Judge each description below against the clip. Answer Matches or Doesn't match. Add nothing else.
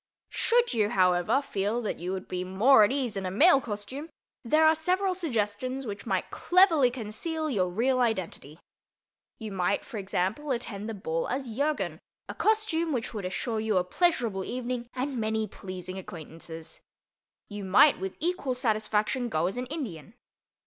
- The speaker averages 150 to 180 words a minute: Matches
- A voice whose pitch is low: Doesn't match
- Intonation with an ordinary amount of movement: Doesn't match